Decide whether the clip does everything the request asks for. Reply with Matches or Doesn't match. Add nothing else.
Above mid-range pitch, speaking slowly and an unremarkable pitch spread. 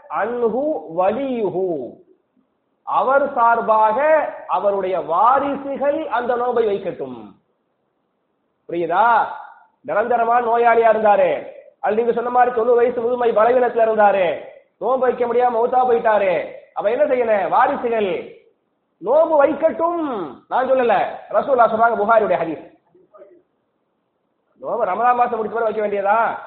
Matches